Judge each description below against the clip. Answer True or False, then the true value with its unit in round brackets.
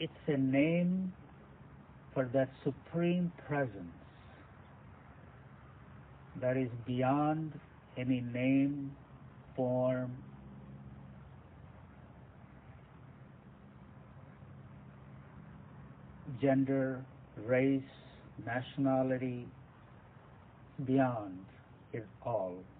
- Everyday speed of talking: False (50 wpm)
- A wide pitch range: True (6.2 semitones)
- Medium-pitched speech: False (130 Hz)